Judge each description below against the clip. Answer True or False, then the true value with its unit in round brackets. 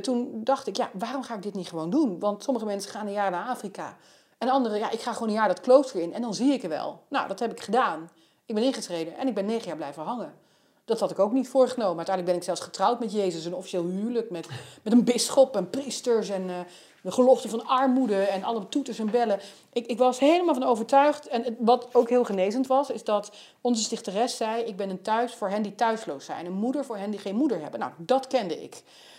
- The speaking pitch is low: False (230 Hz)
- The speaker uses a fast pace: True (250 wpm)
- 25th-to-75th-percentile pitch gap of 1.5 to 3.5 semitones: False (4.2 semitones)